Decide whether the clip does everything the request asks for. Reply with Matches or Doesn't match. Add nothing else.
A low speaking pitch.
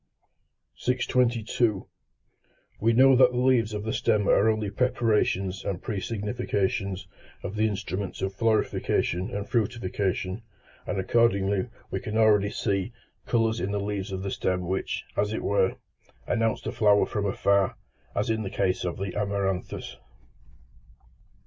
Matches